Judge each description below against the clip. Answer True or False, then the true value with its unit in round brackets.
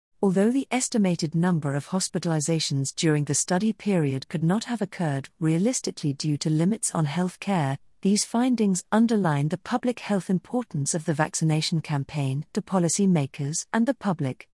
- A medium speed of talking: True (155 wpm)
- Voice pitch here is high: False (180 Hz)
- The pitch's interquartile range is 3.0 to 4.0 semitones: False (4.9 semitones)